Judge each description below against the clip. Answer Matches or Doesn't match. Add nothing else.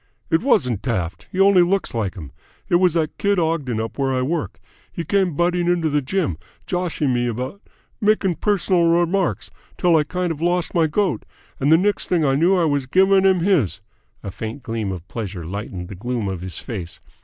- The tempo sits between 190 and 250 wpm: Matches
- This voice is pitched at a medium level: Matches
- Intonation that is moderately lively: Doesn't match